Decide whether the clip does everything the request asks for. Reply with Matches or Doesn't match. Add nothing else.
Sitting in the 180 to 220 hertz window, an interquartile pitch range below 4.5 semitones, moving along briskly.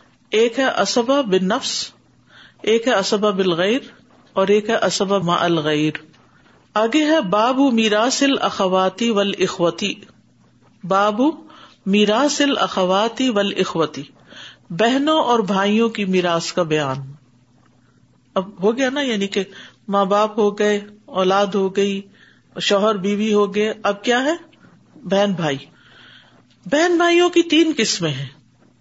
Doesn't match